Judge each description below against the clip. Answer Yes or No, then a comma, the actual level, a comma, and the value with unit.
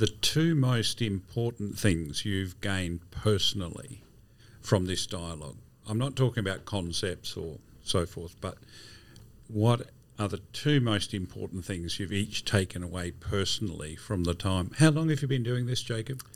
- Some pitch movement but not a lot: Yes, average, 3.8 semitones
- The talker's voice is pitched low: Yes, low, 105 Hz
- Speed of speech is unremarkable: Yes, average, 160 wpm